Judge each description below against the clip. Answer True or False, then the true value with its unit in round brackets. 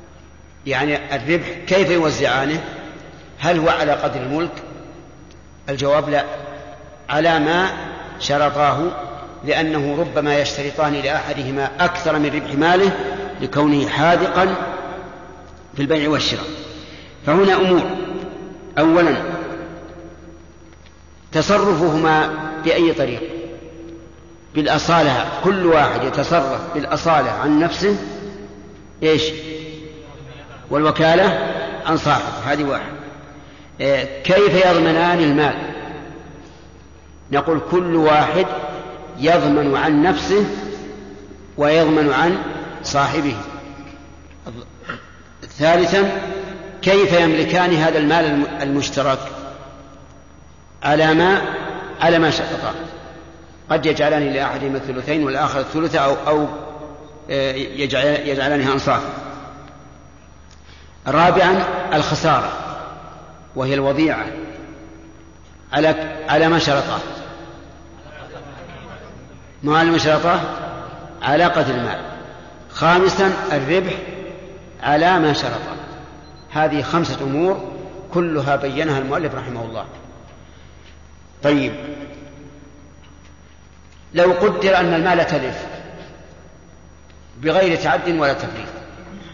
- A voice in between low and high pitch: True (150 Hz)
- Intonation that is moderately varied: True (3.5 semitones)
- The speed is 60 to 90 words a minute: True (80 wpm)